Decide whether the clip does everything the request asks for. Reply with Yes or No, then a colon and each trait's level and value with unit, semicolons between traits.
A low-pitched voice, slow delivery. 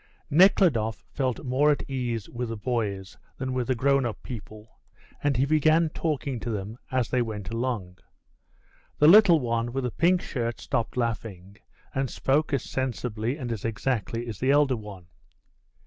No: low, 125 Hz; average, 165 wpm